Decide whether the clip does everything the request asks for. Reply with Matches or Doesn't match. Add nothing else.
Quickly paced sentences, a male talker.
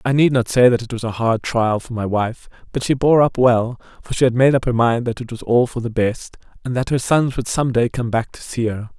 Matches